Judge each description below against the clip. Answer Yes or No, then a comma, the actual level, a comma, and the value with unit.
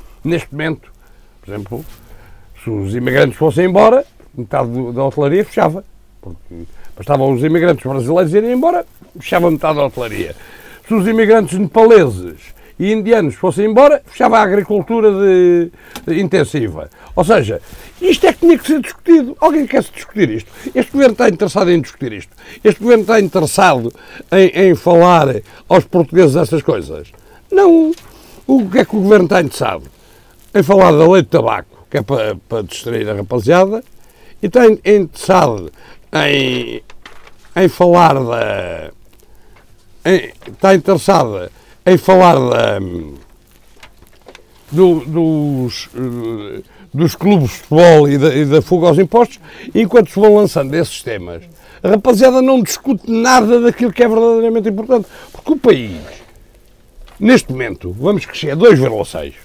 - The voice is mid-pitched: Yes, medium, 180 Hz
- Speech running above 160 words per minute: No, average, 145 wpm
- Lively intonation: Yes, wide, 8.7 semitones